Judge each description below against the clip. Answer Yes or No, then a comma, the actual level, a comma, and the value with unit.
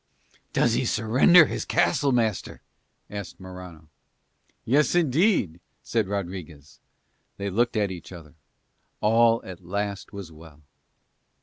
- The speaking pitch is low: Yes, low, 100 Hz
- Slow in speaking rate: Yes, slow, 115 wpm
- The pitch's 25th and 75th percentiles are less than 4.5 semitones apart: No, average, 5.1 semitones